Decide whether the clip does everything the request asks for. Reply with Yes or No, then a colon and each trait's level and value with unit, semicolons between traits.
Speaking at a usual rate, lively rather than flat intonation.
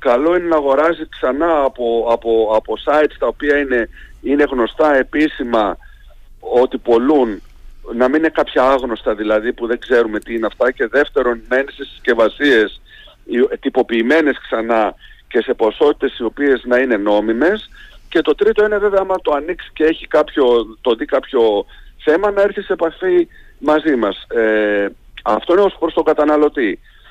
Yes: average, 160 wpm; wide, 6.1 semitones